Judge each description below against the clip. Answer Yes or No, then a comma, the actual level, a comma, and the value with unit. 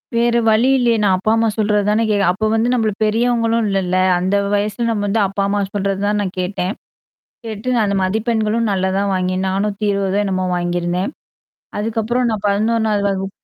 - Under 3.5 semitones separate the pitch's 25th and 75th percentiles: Yes, narrow, 2.5 semitones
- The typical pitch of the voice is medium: No, high, 205 Hz